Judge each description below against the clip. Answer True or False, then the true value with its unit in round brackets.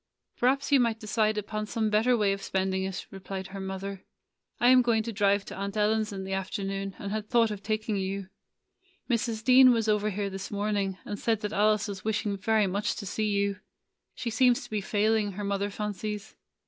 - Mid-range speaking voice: False (210 Hz)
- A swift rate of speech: True (210 wpm)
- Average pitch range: False (1.9 semitones)